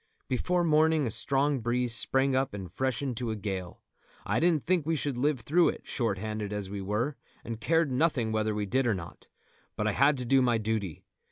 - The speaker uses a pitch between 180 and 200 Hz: No, low, 125 Hz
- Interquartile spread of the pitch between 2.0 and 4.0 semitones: No, average, 4.9 semitones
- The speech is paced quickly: Yes, fast, 210 wpm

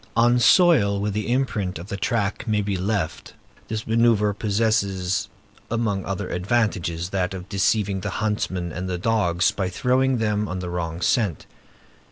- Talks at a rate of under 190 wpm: Yes, average, 160 wpm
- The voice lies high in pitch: No, low, 100 Hz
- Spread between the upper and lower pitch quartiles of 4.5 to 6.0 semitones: No, average, 3.4 semitones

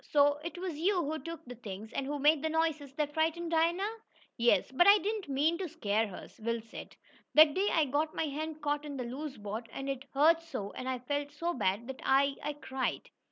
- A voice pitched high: Yes, very high, 290 Hz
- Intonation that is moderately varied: Yes, average, 3.7 semitones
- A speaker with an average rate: No, fast, 225 wpm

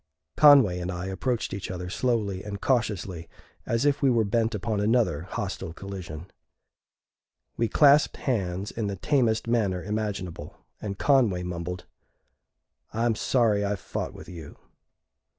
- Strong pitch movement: No, average, 4.3 semitones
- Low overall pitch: Yes, low, 105 Hz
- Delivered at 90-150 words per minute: Yes, slow, 135 wpm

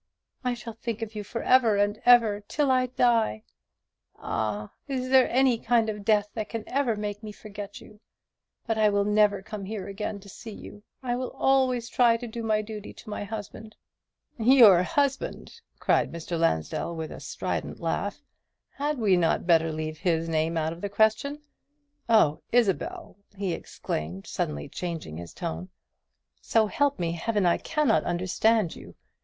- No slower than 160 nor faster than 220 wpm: Yes, average, 170 wpm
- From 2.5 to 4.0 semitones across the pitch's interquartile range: No, average, 5.1 semitones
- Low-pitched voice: No, high, 215 Hz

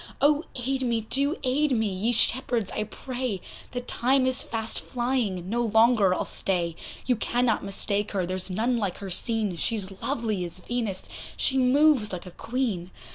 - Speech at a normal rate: Yes, average, 170 wpm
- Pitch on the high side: Yes, high, 225 Hz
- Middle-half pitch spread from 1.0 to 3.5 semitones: No, average, 4.5 semitones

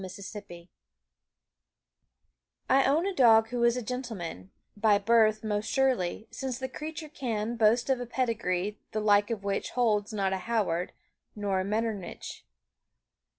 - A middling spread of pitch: Yes, average, 3.4 semitones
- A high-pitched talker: Yes, high, 220 Hz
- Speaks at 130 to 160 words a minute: Yes, average, 150 wpm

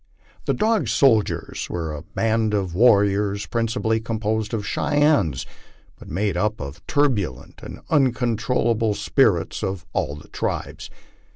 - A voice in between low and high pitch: No, low, 110 Hz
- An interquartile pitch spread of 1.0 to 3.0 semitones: No, average, 3.4 semitones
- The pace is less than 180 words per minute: Yes, slow, 135 wpm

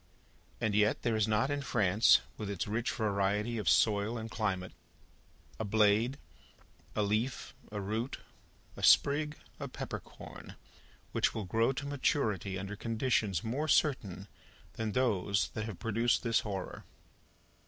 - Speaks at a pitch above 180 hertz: No, low, 110 Hz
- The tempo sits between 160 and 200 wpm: No, average, 140 wpm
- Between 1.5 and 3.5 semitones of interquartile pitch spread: Yes, average, 2.7 semitones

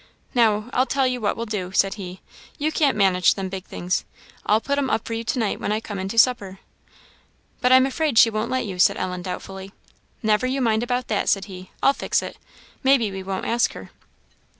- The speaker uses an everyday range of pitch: Yes, average, 4.6 semitones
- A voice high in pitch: Yes, high, 220 Hz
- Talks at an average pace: No, fast, 220 wpm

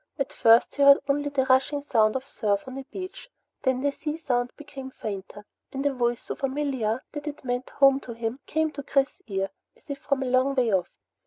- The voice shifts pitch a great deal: No, average, 2.9 semitones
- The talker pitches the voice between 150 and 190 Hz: No, very high, 265 Hz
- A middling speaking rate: No, fast, 220 wpm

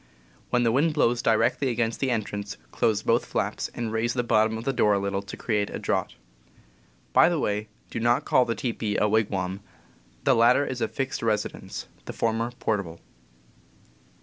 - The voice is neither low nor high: No, low, 115 Hz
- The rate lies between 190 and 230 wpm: Yes, average, 195 wpm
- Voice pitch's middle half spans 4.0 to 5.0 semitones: No, narrow, 2.5 semitones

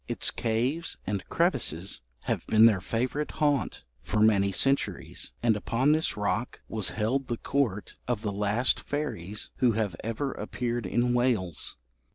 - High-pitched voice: No, low, 115 Hz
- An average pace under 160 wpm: Yes, average, 150 wpm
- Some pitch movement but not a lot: Yes, average, 4.1 semitones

